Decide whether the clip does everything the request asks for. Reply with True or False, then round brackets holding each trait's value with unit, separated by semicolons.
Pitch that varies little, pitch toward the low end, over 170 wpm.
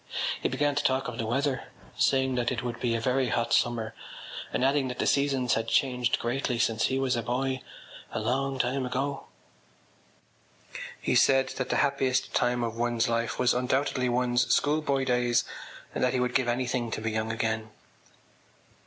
True (2.0 semitones; 125 Hz; 180 wpm)